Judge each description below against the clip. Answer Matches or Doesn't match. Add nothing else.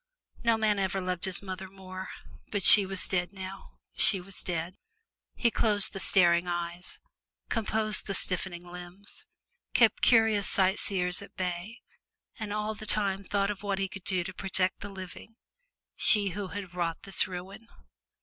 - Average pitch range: Doesn't match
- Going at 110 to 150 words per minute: Doesn't match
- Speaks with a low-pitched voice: Doesn't match